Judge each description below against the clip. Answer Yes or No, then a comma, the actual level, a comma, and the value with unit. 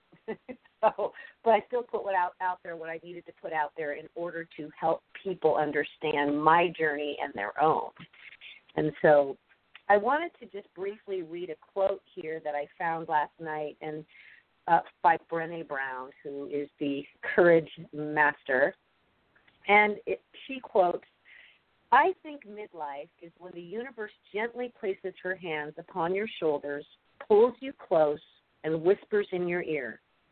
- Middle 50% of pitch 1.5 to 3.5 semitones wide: No, average, 4.9 semitones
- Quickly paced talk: No, average, 155 wpm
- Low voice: No, medium, 170 Hz